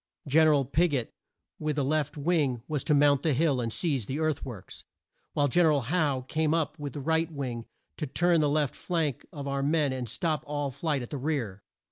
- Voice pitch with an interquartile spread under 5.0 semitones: Yes, average, 2.9 semitones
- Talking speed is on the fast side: Yes, fast, 225 wpm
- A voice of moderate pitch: Yes, medium, 145 Hz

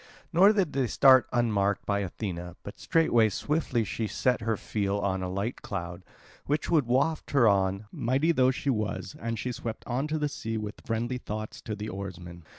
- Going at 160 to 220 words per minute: Yes, average, 190 wpm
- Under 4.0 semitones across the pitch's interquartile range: No, average, 4.7 semitones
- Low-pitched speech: Yes, low, 115 Hz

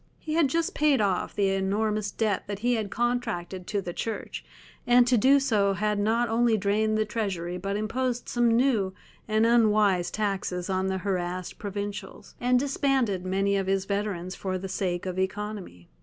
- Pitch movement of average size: Yes, average, 3.4 semitones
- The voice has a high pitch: Yes, high, 205 Hz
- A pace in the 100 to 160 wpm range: No, average, 175 wpm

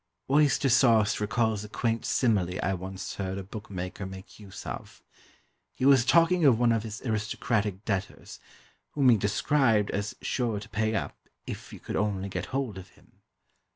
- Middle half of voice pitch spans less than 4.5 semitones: Yes, average, 3.6 semitones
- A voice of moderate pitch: No, low, 110 Hz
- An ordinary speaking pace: Yes, average, 170 wpm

